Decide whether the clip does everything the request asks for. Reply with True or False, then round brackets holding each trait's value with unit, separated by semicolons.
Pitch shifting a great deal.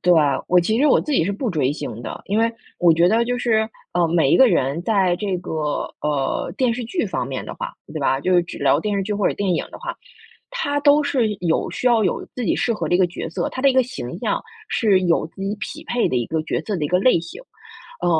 True (5.7 semitones)